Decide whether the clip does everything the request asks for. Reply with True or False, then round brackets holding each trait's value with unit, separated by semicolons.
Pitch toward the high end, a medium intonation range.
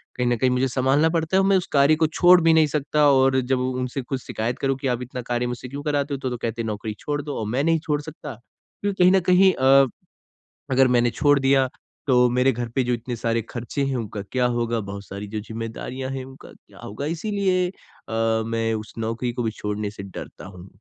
False (130 Hz; 3.8 semitones)